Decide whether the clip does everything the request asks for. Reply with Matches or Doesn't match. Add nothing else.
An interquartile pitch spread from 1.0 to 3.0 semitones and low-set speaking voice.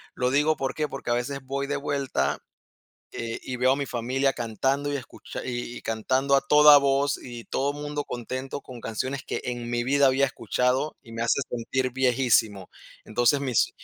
Matches